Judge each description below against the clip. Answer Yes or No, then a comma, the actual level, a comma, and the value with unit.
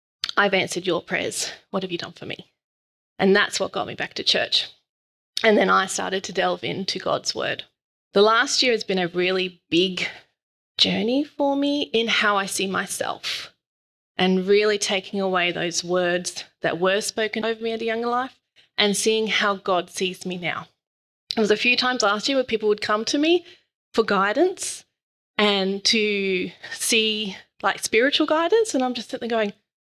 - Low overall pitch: No, high, 205 Hz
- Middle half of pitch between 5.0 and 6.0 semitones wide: No, average, 3.8 semitones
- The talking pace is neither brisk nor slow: Yes, average, 185 wpm